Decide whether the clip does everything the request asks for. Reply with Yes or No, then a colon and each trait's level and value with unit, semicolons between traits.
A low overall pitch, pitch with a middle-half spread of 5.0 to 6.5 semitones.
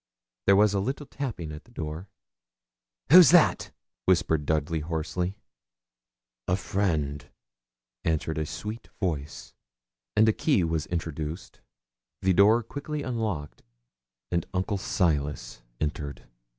Yes: very low, 90 Hz; wide, 5.5 semitones